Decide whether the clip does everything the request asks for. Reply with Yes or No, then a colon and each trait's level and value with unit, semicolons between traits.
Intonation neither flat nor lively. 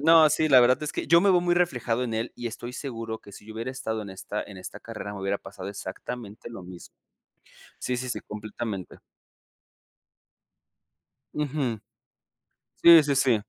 Yes: average, 5.0 semitones